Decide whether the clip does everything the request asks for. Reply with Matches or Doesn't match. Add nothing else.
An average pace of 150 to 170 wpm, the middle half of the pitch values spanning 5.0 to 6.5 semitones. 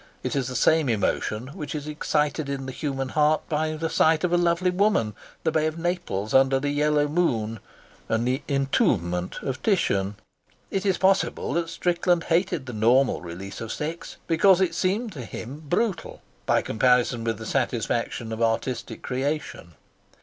Matches